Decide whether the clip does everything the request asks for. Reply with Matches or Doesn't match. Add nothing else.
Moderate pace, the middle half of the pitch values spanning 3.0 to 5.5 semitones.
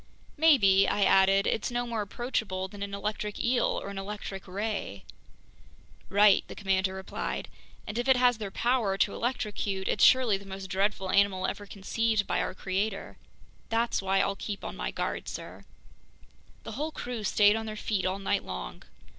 Doesn't match